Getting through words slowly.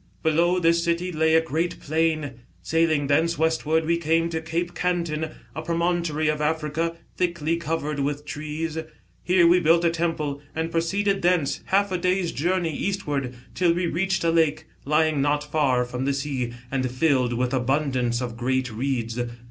No: average, 165 wpm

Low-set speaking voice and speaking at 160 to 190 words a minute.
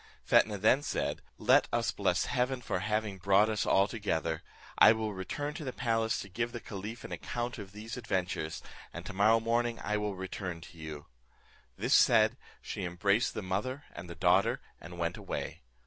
Yes: low, 105 Hz; average, 180 wpm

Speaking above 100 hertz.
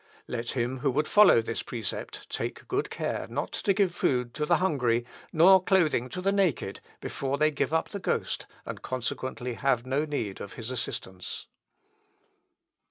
Yes: low, 135 Hz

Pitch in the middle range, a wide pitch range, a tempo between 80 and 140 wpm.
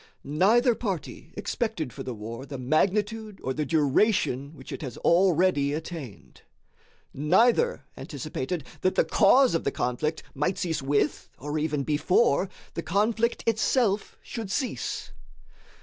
Yes: medium, 165 Hz; wide, 6.8 semitones; slow, 135 wpm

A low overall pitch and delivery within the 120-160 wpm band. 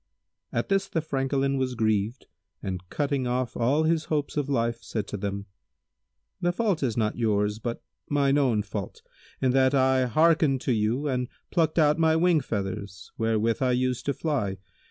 No: low, 130 Hz; average, 175 wpm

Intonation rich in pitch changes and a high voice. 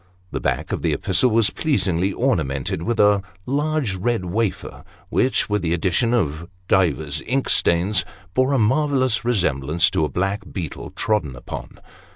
No: wide, 6.3 semitones; low, 100 Hz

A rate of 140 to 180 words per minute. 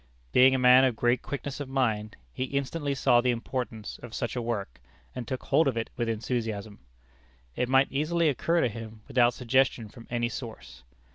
No: average, 190 wpm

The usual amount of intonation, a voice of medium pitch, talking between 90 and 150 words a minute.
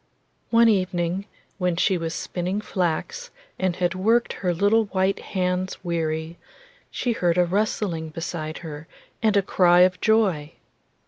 Yes: average, 3.0 semitones; medium, 180 Hz; average, 140 wpm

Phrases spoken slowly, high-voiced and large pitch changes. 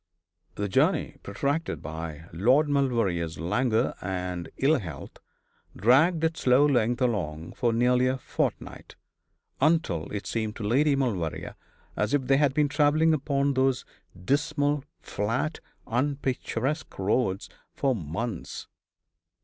No: slow, 120 wpm; low, 125 Hz; wide, 6.6 semitones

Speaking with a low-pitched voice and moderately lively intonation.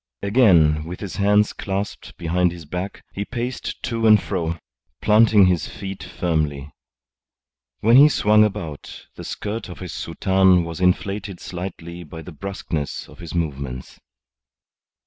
Yes: very low, 90 Hz; average, 3.8 semitones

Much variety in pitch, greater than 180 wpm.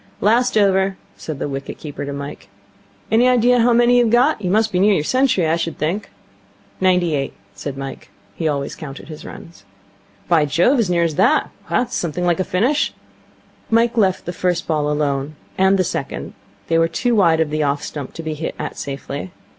Yes: wide, 6.3 semitones; average, 200 wpm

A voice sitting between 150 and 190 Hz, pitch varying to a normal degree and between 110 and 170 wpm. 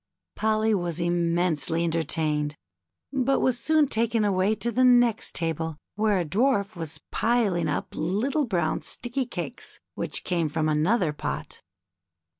No: medium, 185 Hz; wide, 6.3 semitones; slow, 135 wpm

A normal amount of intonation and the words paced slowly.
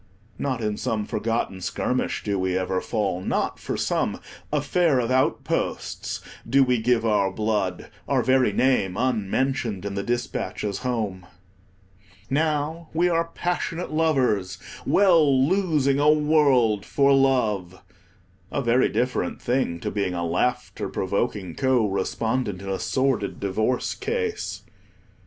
No: wide, 5.8 semitones; slow, 130 wpm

